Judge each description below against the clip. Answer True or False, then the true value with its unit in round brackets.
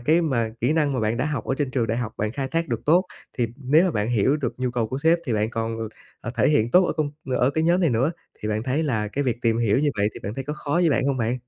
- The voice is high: False (130 Hz)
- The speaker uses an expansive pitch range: False (4.8 semitones)